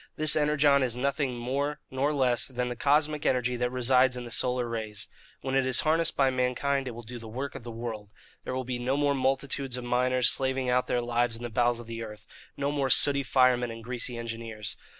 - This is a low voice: Yes, low, 125 Hz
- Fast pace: Yes, fast, 225 wpm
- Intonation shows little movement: Yes, narrow, 2.3 semitones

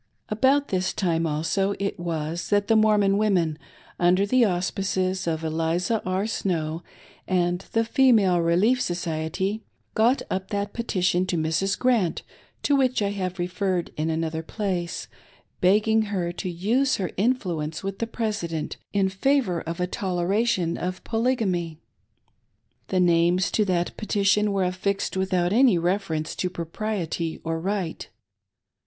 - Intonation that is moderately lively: Yes, average, 3.5 semitones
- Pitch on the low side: No, medium, 185 Hz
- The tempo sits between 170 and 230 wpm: No, average, 140 wpm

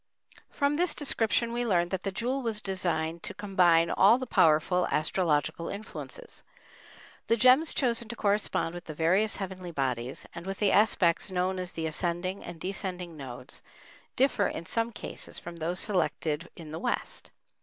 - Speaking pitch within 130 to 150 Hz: No, medium, 185 Hz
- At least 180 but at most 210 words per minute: No, average, 165 wpm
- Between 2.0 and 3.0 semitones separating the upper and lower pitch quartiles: No, average, 4.5 semitones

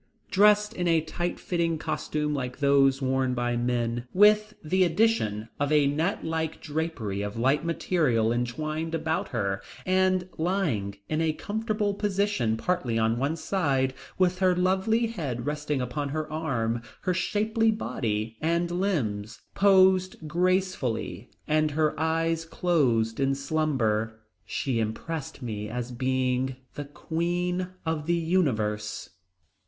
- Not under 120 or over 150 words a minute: Yes, slow, 135 wpm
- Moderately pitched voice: Yes, medium, 155 Hz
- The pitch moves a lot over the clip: Yes, wide, 6.6 semitones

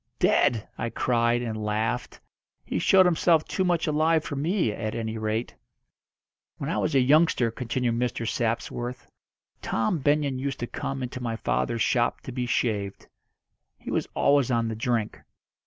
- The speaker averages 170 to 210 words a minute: No, average, 160 wpm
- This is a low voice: Yes, low, 125 Hz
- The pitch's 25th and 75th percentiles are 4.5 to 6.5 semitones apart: No, average, 3.9 semitones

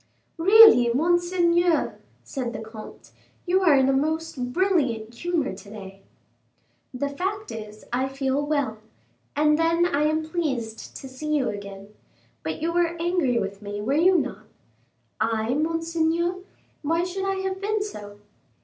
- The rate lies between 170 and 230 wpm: No, average, 150 wpm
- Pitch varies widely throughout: Yes, wide, 6.6 semitones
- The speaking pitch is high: Yes, very high, 300 Hz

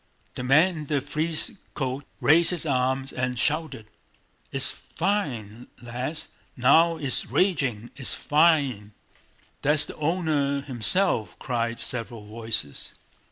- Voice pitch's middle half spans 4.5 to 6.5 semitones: Yes, average, 4.8 semitones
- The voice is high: No, medium, 140 Hz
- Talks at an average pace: No, slow, 115 wpm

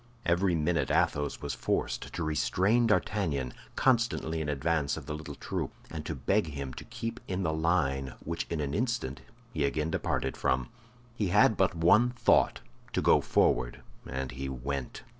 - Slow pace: No, average, 165 wpm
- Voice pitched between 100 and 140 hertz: No, very low, 80 Hz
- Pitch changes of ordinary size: No, wide, 5.7 semitones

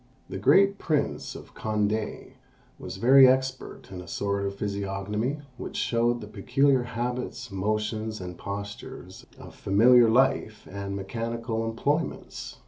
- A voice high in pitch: No, low, 110 Hz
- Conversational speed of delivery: No, slow, 130 wpm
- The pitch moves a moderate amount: Yes, average, 3.9 semitones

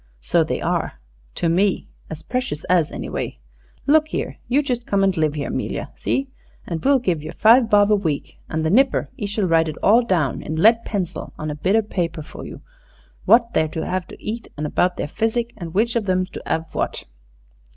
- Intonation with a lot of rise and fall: Yes, wide, 6.3 semitones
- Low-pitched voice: No, high, 190 Hz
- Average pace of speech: No, fast, 215 wpm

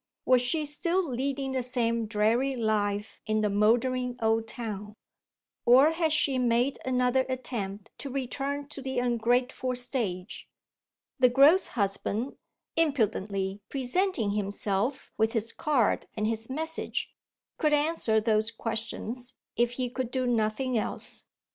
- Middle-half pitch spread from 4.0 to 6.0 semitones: No, average, 3.5 semitones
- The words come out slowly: Yes, slow, 130 wpm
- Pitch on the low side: No, high, 245 Hz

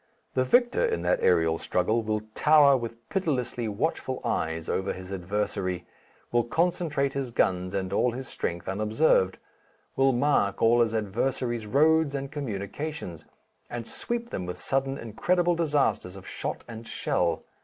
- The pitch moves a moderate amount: No, wide, 6.6 semitones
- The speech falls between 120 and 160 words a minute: Yes, average, 145 wpm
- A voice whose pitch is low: Yes, low, 115 Hz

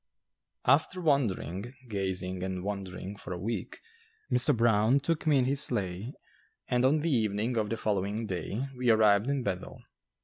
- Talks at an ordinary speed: Yes, average, 160 wpm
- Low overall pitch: Yes, low, 110 Hz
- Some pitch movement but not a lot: Yes, average, 4.6 semitones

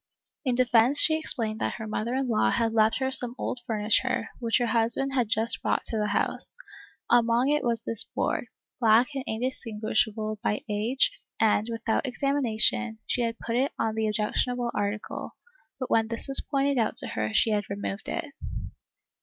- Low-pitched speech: No, high, 230 Hz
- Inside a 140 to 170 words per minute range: No, average, 180 wpm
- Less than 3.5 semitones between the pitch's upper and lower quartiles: Yes, average, 2.7 semitones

